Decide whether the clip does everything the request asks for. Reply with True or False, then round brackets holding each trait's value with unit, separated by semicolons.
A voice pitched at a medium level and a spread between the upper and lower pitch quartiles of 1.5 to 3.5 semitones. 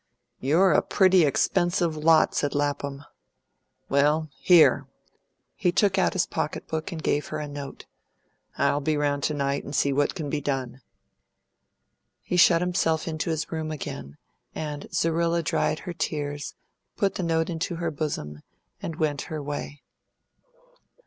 True (155 Hz; 2.6 semitones)